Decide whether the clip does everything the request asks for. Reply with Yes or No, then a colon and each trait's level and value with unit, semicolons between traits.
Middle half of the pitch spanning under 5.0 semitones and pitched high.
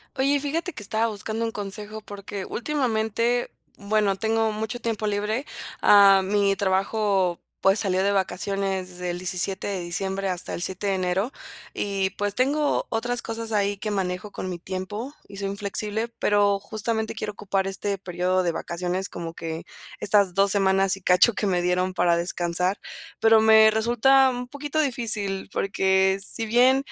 Yes: average, 2.7 semitones; high, 200 Hz